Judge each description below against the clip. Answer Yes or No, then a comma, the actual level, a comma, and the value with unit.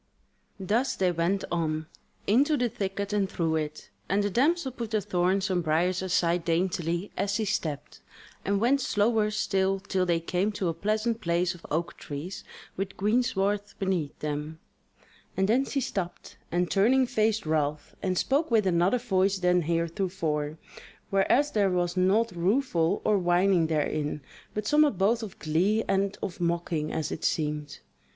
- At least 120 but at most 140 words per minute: No, average, 160 wpm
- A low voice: No, high, 190 Hz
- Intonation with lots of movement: No, average, 3.9 semitones